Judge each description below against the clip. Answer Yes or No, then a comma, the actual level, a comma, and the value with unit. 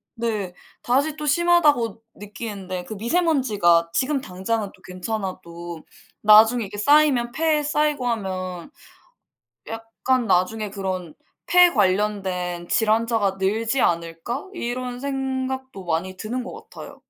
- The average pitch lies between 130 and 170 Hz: No, high, 225 Hz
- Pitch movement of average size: No, wide, 5.8 semitones